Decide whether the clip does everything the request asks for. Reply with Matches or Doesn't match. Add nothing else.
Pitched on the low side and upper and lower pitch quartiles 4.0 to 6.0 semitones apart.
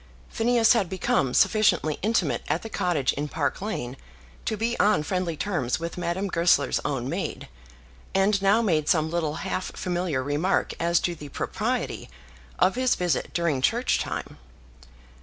Doesn't match